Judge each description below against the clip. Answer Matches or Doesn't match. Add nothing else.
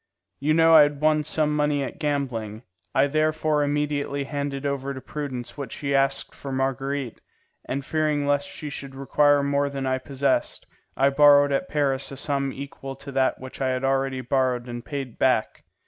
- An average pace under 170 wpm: Doesn't match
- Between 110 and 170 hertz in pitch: Matches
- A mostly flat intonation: Matches